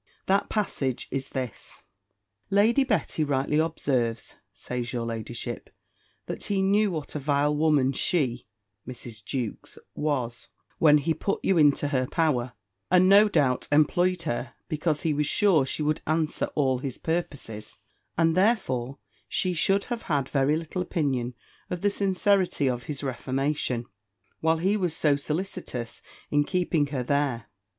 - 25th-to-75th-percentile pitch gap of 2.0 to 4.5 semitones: No, average, 5.3 semitones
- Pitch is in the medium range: Yes, medium, 150 Hz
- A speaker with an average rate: Yes, average, 145 wpm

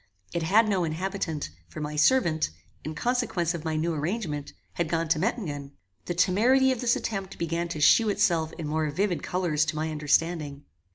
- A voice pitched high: No, medium, 170 Hz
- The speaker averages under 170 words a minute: No, average, 180 wpm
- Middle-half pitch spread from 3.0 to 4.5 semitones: Yes, average, 4.1 semitones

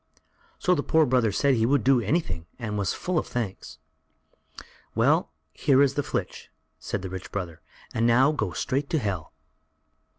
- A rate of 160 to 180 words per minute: Yes, average, 170 wpm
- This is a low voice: Yes, low, 120 Hz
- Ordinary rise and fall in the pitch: No, wide, 5.9 semitones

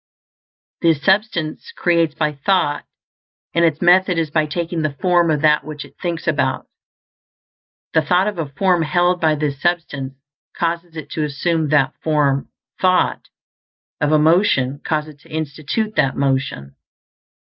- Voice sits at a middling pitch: Yes, medium, 155 Hz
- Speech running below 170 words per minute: Yes, average, 155 wpm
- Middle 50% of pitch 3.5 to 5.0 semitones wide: No, average, 2.9 semitones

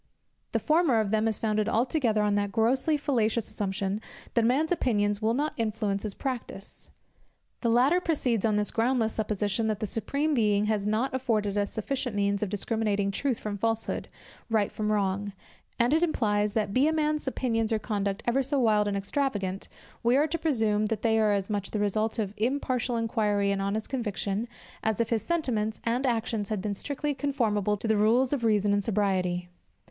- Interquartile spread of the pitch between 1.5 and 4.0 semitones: Yes, average, 3.3 semitones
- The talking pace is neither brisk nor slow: Yes, average, 190 wpm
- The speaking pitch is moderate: No, high, 220 Hz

